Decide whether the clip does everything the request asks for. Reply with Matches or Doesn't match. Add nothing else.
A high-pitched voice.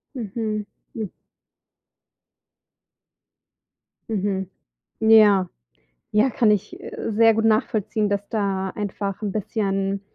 Matches